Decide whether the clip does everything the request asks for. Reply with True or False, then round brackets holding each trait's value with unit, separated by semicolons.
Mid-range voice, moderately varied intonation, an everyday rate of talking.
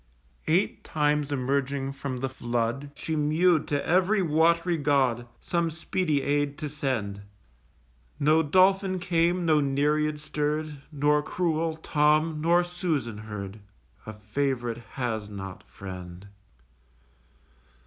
False (150 Hz; 4.2 semitones; 115 wpm)